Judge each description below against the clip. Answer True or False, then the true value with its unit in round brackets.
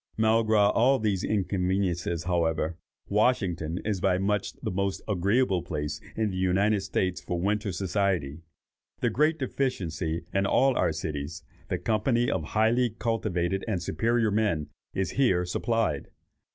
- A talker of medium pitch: False (95 Hz)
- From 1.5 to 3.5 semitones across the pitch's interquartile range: False (4.0 semitones)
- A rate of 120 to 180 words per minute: True (140 wpm)